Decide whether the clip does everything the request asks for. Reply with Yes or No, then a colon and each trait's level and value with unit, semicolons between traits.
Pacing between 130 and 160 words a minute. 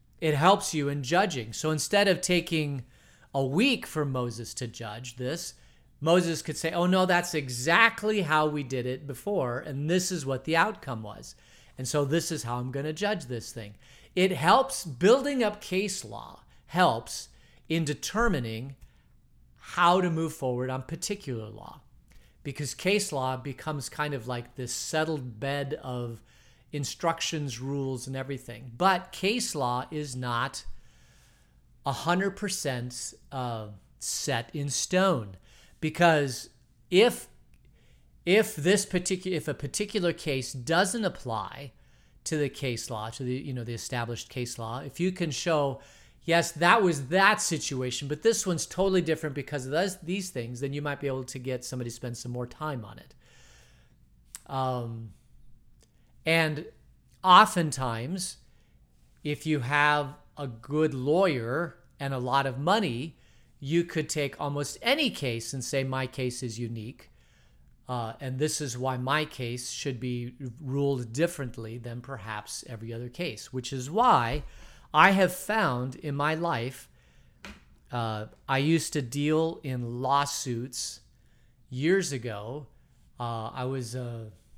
Yes: average, 150 wpm